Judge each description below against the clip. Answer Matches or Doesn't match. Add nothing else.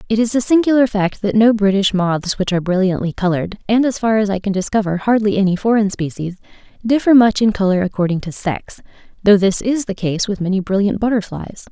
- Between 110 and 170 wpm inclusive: Doesn't match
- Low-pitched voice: Doesn't match